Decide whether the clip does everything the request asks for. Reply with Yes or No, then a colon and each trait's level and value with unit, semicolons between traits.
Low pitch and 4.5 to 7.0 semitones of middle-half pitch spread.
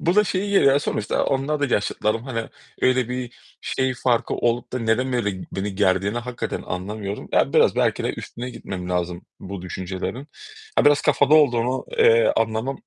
Yes: low, 120 Hz; average, 4.9 semitones